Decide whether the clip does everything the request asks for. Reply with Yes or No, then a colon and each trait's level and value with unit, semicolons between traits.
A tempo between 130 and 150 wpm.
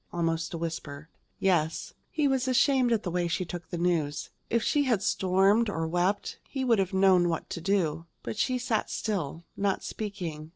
No: average, 190 wpm